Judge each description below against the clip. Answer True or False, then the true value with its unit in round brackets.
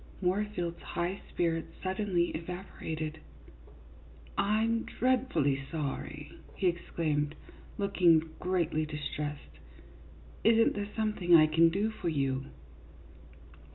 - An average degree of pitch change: True (4.5 semitones)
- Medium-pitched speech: True (170 Hz)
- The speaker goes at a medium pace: False (100 wpm)